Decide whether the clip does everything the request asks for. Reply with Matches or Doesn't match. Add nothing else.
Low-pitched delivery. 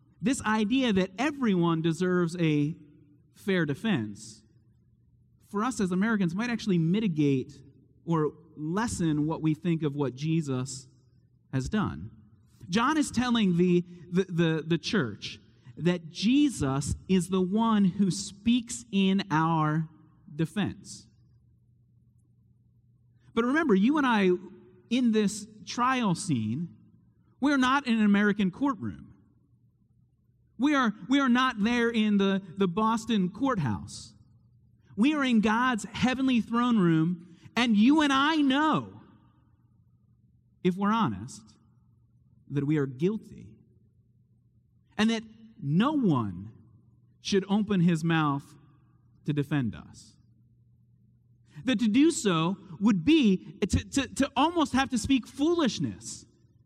Doesn't match